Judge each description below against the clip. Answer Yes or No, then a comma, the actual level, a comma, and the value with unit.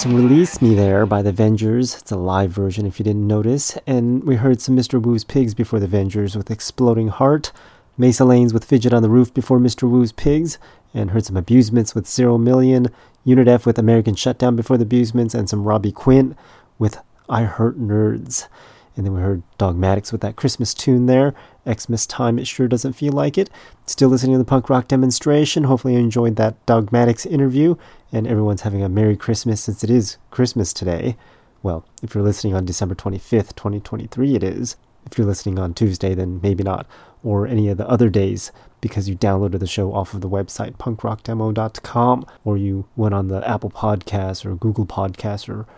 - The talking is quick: No, average, 195 wpm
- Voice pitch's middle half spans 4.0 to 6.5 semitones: No, average, 3.6 semitones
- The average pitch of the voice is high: No, low, 115 Hz